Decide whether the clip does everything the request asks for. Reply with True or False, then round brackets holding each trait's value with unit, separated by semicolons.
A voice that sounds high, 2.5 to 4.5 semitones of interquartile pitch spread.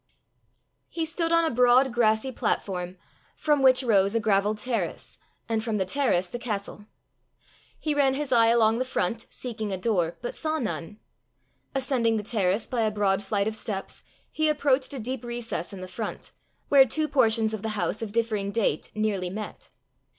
True (225 Hz; 3.9 semitones)